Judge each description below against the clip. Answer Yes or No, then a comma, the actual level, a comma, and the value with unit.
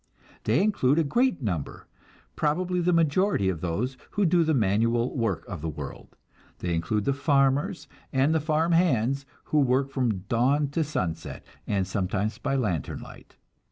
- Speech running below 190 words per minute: Yes, average, 160 wpm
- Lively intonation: Yes, wide, 7.1 semitones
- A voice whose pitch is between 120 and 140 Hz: Yes, low, 135 Hz